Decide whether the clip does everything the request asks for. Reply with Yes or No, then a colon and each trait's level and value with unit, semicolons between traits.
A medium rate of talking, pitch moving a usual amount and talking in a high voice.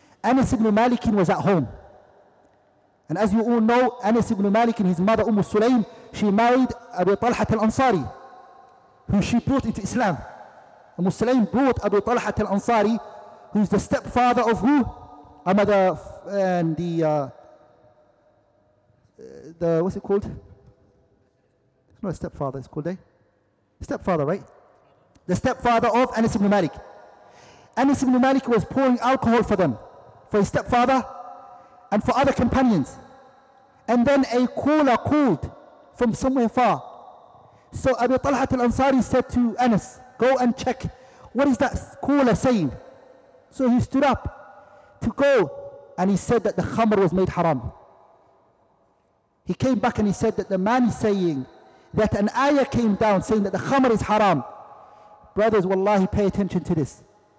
Yes: average, 155 wpm; average, 4.6 semitones; high, 225 Hz